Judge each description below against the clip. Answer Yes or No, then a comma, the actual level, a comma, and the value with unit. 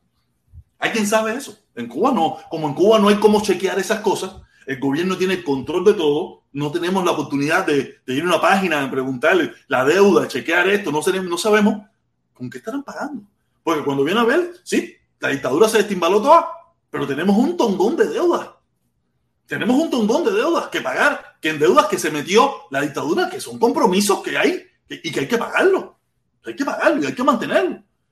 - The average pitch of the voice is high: Yes, high, 205 Hz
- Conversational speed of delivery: No, fast, 200 wpm